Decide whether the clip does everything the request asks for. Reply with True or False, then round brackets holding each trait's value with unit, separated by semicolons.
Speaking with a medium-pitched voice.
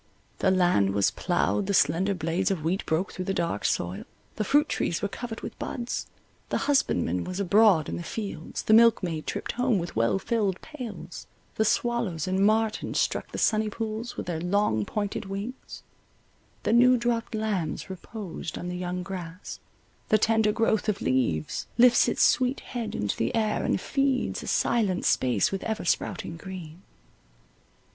False (195 Hz)